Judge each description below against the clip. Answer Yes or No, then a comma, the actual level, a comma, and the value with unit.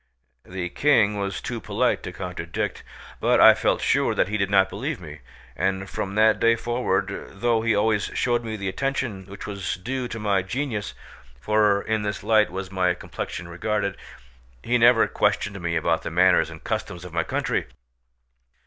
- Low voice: Yes, low, 100 Hz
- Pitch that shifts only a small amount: No, average, 3.3 semitones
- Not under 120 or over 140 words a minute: No, average, 175 wpm